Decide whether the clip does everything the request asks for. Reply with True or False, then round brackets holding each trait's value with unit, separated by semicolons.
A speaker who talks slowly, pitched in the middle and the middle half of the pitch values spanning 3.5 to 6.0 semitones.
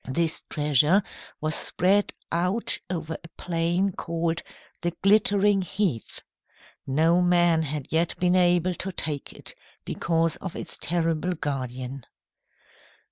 False (120 wpm; 170 Hz; 2.6 semitones)